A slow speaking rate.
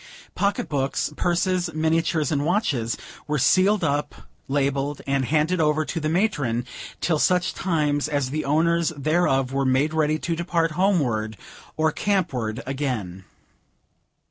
Yes: slow, 130 wpm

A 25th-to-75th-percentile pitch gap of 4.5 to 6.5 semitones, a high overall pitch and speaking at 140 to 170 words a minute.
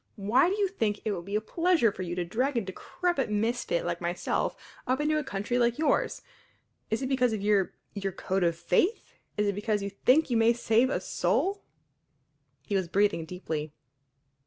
No: wide, 5.4 semitones; high, 220 Hz; average, 195 wpm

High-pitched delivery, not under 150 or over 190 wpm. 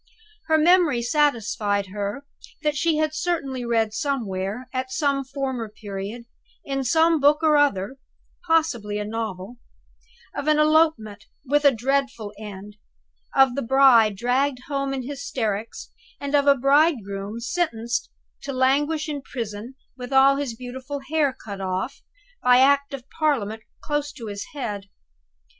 No: very high, 260 Hz; average, 140 wpm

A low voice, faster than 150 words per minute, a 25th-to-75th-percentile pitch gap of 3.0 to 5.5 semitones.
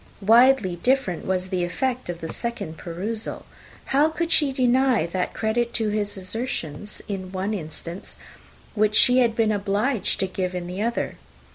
No: high, 210 Hz; average, 160 wpm; average, 4.8 semitones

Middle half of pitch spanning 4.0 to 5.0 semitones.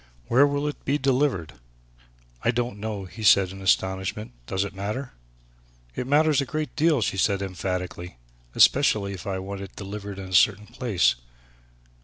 No: wide, 5.6 semitones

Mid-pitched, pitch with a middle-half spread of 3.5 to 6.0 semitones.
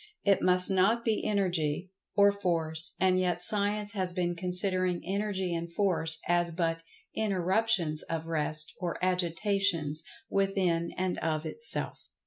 No: medium, 180 Hz; average, 2.9 semitones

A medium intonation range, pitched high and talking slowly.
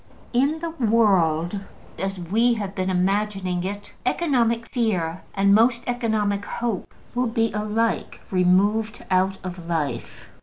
Yes: average, 3.8 semitones; high, 205 Hz; slow, 125 wpm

